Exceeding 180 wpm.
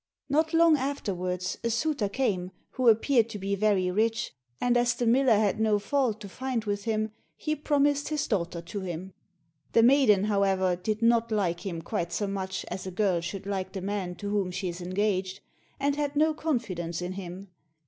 Yes: average, 190 wpm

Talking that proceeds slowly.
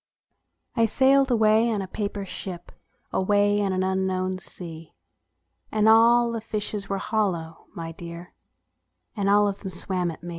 No: average, 155 wpm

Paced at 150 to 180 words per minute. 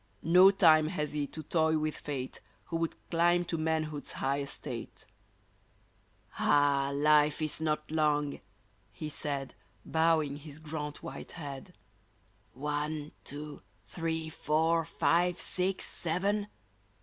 No: slow, 135 wpm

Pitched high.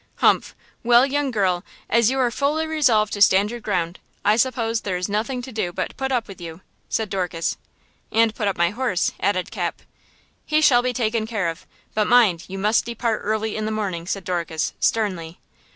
Yes: high, 215 Hz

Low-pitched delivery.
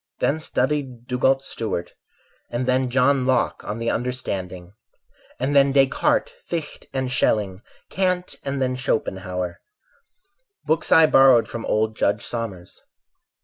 Yes: low, 125 Hz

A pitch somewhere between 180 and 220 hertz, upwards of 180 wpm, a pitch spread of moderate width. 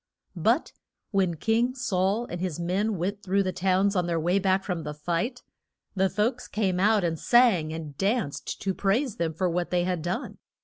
Yes: high, 190 Hz; average, 190 wpm; average, 3.3 semitones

